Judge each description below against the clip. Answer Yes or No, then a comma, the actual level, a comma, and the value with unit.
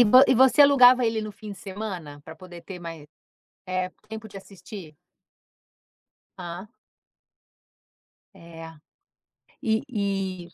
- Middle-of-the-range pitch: No, high, 195 Hz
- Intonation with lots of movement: No, average, 4.1 semitones